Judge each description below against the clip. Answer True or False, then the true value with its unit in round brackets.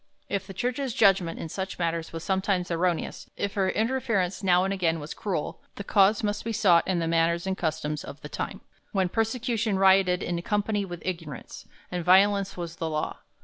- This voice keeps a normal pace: True (190 wpm)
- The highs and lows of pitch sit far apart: False (3.1 semitones)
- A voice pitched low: False (190 Hz)